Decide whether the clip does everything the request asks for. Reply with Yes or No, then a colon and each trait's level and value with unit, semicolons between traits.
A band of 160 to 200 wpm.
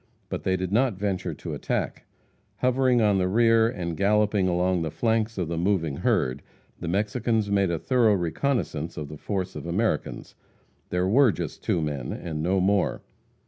Yes: average, 175 wpm